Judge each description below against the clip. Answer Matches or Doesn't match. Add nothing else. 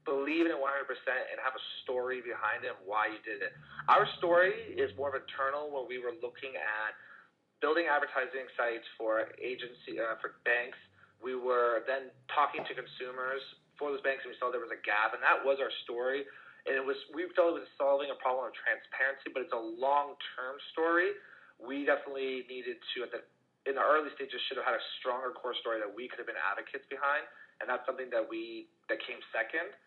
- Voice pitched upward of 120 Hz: Matches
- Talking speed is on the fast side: Matches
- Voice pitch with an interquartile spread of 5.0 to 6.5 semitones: Matches